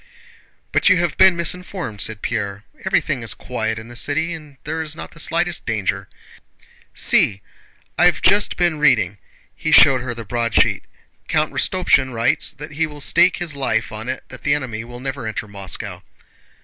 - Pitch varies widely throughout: Yes, wide, 6.5 semitones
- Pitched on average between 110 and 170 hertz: Yes, low, 135 Hz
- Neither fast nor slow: Yes, average, 175 wpm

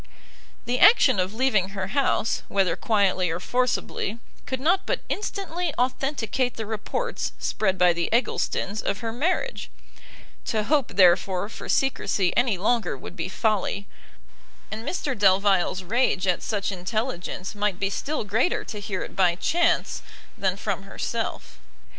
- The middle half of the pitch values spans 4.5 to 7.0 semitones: Yes, average, 4.8 semitones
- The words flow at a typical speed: Yes, average, 145 wpm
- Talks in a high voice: Yes, high, 210 Hz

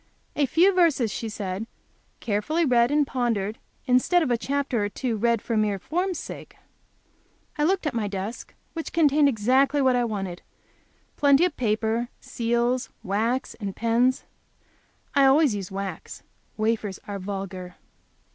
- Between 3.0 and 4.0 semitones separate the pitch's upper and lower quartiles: No, average, 5.2 semitones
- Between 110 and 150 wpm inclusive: Yes, average, 145 wpm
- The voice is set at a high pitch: Yes, high, 235 Hz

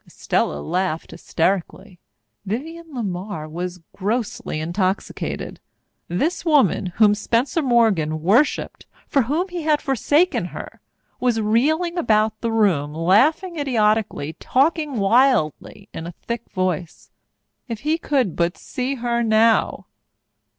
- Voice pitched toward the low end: No, high, 225 Hz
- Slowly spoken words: Yes, slow, 115 wpm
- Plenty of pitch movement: Yes, wide, 6.8 semitones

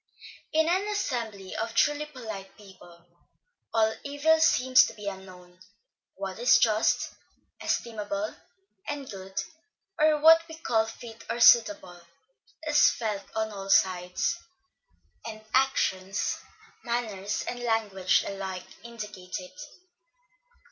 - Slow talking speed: Yes, slow, 115 wpm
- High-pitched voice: Yes, high, 220 Hz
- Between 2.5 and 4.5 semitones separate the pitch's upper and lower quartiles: No, average, 4.9 semitones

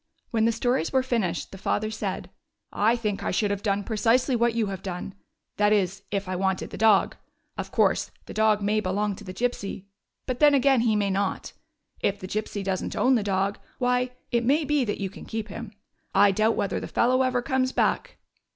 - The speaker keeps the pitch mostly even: No, average, 3.6 semitones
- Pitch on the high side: Yes, high, 215 Hz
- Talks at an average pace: No, fast, 215 wpm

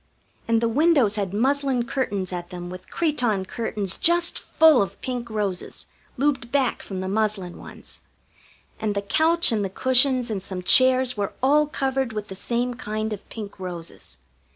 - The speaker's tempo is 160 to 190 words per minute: Yes, average, 170 wpm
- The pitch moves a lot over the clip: No, average, 4.9 semitones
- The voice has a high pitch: Yes, high, 230 Hz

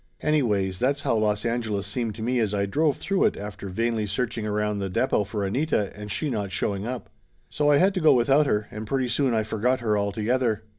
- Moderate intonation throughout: Yes, average, 3.8 semitones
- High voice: No, low, 110 Hz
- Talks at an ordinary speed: No, fast, 220 wpm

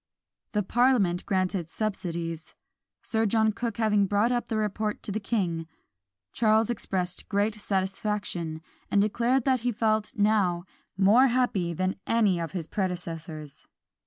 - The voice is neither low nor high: No, high, 205 Hz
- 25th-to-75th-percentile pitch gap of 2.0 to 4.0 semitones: Yes, average, 3.7 semitones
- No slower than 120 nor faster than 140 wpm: Yes, slow, 135 wpm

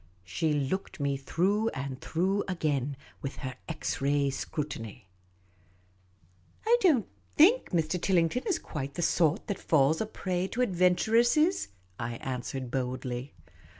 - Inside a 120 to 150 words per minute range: Yes, average, 145 wpm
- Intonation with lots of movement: Yes, wide, 6.5 semitones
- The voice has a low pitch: No, medium, 150 Hz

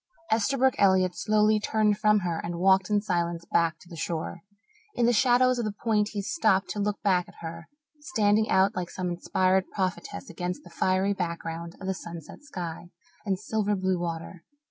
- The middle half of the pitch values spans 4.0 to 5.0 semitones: No, average, 3.4 semitones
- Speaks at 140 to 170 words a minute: No, average, 185 wpm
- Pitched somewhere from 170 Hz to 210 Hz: Yes, high, 190 Hz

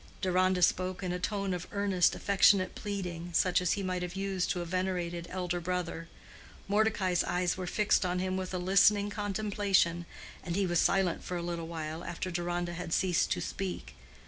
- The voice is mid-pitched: Yes, medium, 180 Hz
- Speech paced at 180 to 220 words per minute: Yes, average, 185 wpm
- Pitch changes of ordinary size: No, narrow, 1.7 semitones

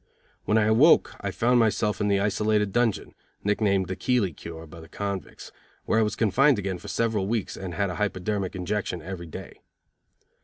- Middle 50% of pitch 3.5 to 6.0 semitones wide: No, average, 2.7 semitones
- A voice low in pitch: Yes, low, 100 Hz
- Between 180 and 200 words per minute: Yes, average, 185 wpm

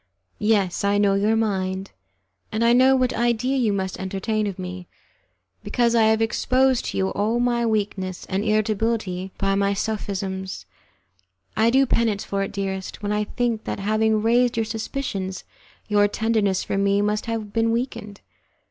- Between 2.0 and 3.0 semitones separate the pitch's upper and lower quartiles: Yes, narrow, 2.6 semitones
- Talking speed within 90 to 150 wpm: No, average, 165 wpm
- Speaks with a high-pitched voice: Yes, high, 210 Hz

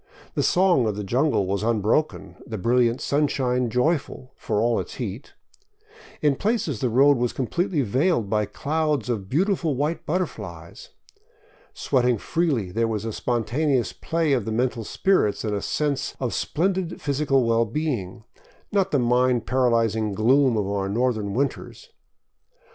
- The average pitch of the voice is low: Yes, low, 125 Hz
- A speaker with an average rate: Yes, average, 155 wpm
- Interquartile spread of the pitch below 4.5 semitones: No, average, 5.0 semitones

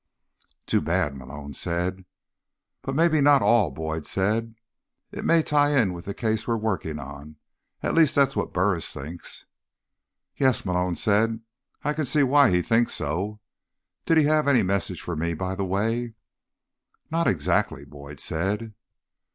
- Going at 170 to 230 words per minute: No, average, 155 wpm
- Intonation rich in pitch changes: Yes, wide, 7.5 semitones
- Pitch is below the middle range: Yes, low, 100 Hz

